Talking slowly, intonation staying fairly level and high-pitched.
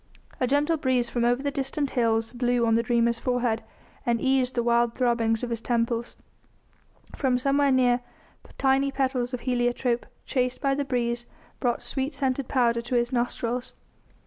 No: average, 165 wpm; narrow, 1.9 semitones; high, 245 Hz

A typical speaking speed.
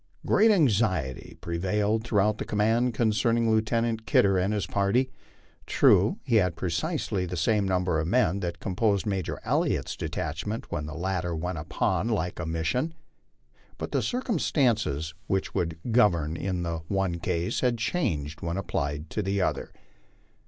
Yes: average, 150 wpm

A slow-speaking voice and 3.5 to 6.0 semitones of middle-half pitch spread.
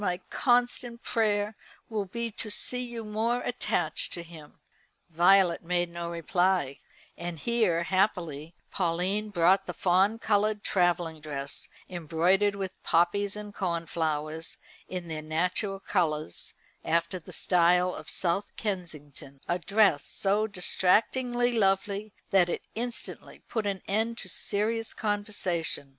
Yes: slow, 125 wpm; average, 3.8 semitones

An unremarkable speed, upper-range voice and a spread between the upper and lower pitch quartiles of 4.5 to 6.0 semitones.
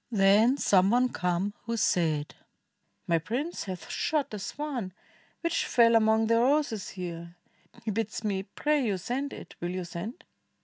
Yes: average, 160 wpm; high, 220 Hz; average, 5.1 semitones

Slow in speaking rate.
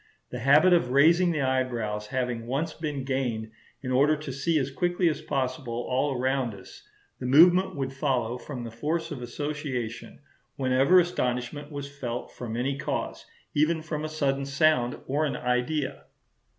No: average, 165 wpm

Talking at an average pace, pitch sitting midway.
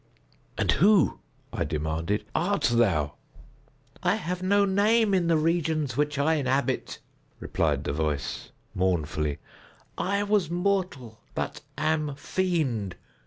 No: slow, 120 wpm; medium, 155 Hz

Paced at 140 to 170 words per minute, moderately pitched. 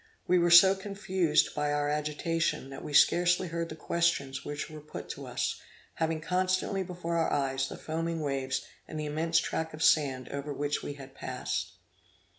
No: average, 180 wpm; medium, 160 Hz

